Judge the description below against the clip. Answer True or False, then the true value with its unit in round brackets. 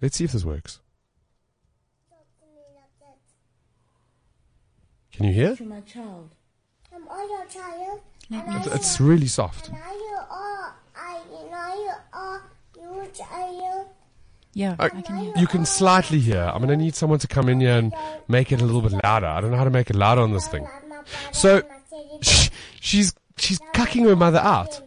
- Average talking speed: False (130 wpm)